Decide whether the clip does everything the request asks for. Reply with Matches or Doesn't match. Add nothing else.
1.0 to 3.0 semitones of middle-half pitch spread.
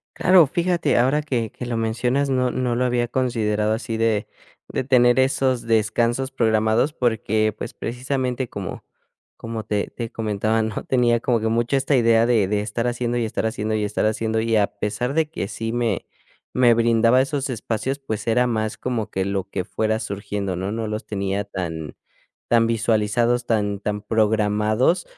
Matches